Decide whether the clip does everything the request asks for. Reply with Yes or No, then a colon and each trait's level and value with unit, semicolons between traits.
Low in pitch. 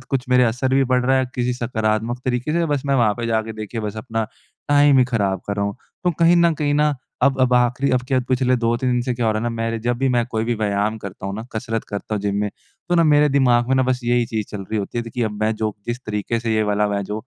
Yes: low, 120 Hz